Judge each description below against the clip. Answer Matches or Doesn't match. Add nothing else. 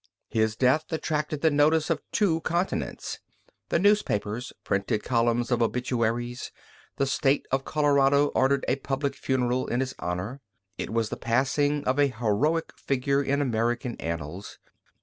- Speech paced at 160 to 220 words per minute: Doesn't match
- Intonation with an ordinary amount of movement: Matches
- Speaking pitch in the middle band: Doesn't match